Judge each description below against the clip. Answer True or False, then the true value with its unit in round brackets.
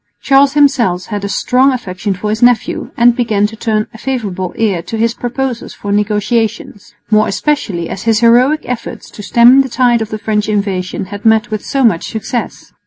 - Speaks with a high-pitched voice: True (220 Hz)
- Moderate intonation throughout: True (3.0 semitones)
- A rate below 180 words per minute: False (185 wpm)